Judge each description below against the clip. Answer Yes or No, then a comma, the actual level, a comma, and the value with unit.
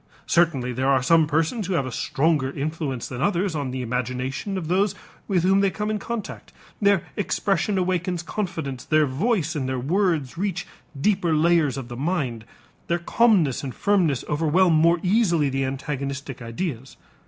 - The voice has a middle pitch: Yes, medium, 160 Hz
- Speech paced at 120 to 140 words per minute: No, average, 165 wpm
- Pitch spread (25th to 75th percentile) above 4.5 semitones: Yes, wide, 5.6 semitones